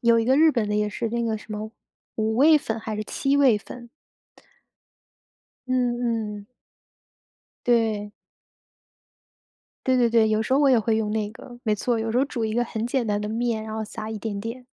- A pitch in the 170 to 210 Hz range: No, high, 225 Hz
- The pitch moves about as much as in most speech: No, narrow, 2.0 semitones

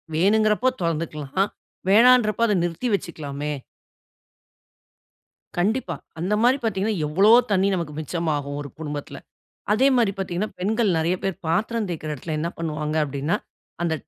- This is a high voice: No, medium, 175 Hz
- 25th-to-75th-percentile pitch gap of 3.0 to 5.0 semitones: No, wide, 5.5 semitones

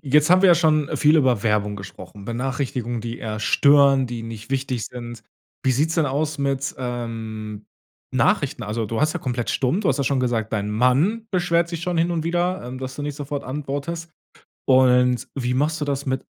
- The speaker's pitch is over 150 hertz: No, low, 130 Hz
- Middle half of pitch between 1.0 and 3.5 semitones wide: No, average, 4.4 semitones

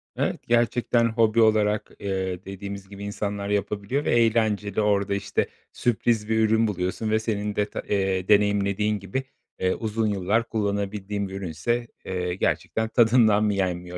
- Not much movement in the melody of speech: Yes, narrow, 2.1 semitones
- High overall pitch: No, low, 105 Hz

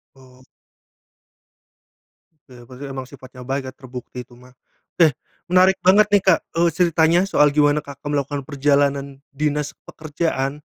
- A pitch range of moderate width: Yes, average, 3.3 semitones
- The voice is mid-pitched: Yes, medium, 145 Hz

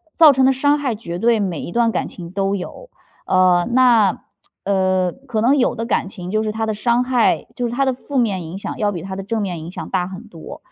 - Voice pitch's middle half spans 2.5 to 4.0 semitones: No, average, 4.7 semitones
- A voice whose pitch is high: Yes, high, 215 Hz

